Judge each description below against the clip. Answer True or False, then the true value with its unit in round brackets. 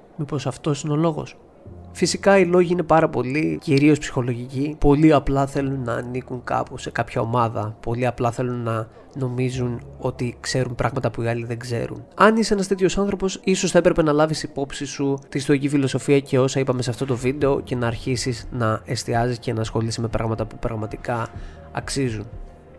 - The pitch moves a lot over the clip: False (3.9 semitones)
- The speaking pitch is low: True (130 Hz)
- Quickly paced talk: True (185 wpm)